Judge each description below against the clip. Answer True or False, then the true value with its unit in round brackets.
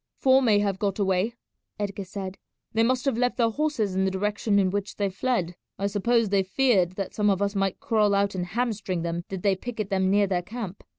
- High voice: True (200 Hz)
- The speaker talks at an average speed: False (225 wpm)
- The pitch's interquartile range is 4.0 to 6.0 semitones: False (2.8 semitones)